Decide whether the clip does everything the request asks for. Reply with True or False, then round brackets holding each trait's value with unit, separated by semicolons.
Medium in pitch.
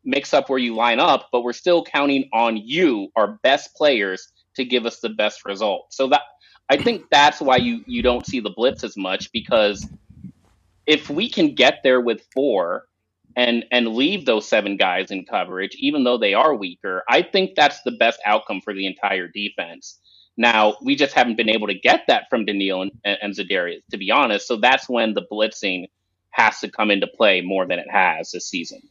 False (120 Hz)